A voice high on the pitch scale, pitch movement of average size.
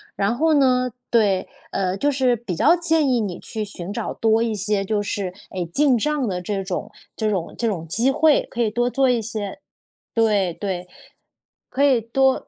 Yes: high, 220 Hz; average, 4.8 semitones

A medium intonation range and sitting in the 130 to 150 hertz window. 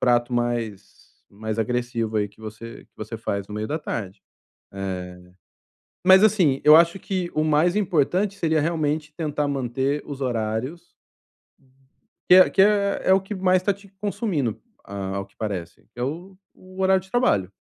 No: wide, 9.0 semitones; medium, 140 Hz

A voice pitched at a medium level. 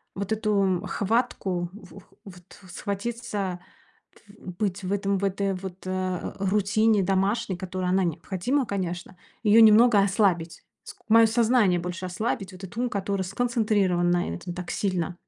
No: high, 195 Hz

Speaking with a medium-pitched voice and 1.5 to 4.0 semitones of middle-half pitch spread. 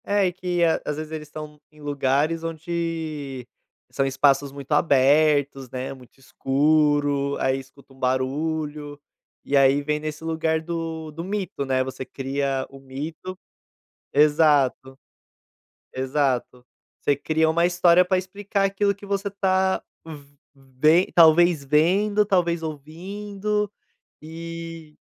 Yes: medium, 155 Hz; average, 3.6 semitones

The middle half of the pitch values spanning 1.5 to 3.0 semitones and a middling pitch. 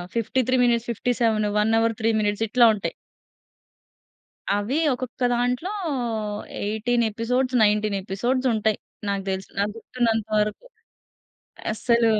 No: narrow, 2.6 semitones; high, 225 Hz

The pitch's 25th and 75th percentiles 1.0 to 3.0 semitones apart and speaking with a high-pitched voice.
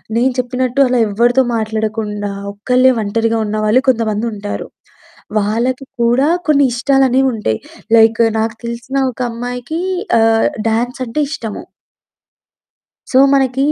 Yes: average, 2.7 semitones; high, 235 Hz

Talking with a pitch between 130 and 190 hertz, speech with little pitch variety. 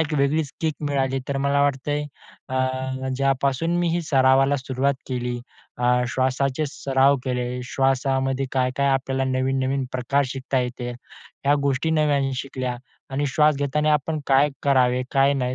Yes: low, 135 Hz; narrow, 1.4 semitones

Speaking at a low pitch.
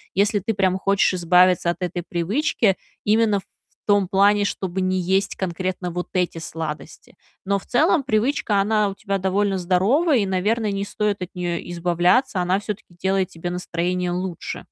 No: high, 190 Hz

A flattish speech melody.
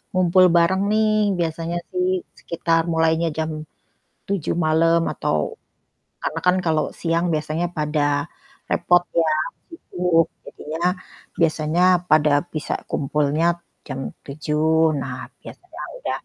Yes: narrow, 2.3 semitones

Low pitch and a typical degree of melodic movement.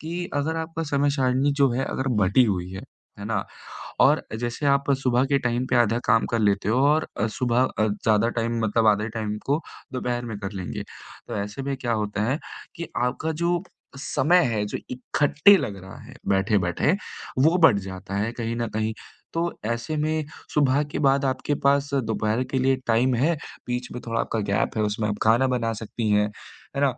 Yes: low, 120 Hz; average, 4.4 semitones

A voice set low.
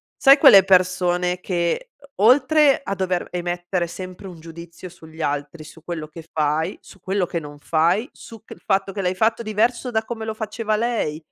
No: medium, 185 Hz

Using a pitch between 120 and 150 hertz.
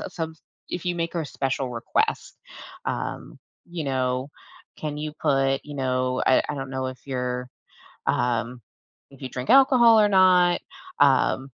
Yes: low, 135 Hz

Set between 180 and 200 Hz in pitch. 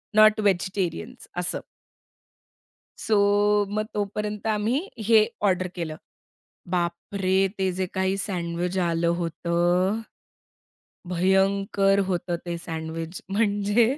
Yes: high, 190 Hz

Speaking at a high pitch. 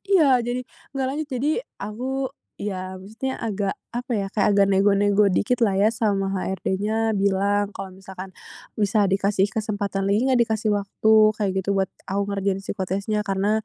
Yes: high, 205 Hz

